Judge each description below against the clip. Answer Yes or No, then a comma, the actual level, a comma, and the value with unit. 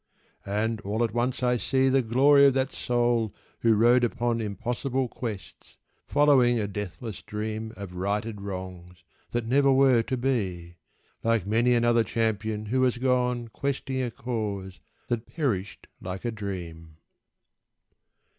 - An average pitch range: Yes, average, 3.4 semitones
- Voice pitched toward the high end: No, low, 115 Hz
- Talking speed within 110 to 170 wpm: Yes, average, 140 wpm